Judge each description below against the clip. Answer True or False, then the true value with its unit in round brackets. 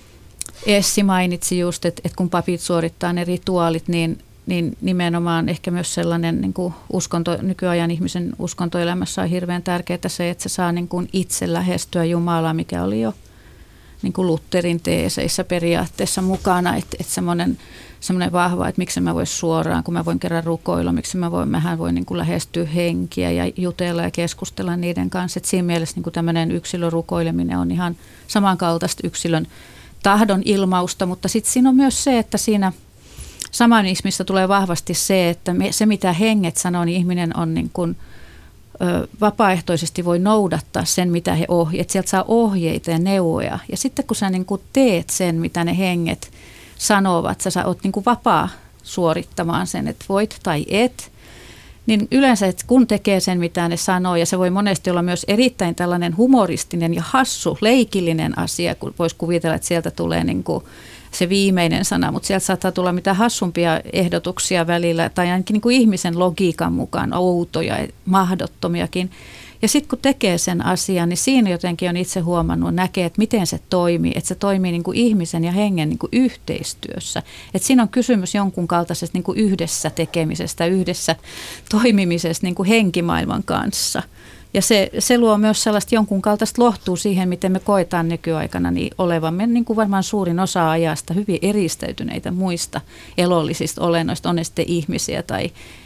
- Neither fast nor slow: False (170 wpm)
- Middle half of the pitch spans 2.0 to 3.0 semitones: True (2.6 semitones)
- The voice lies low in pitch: False (180 Hz)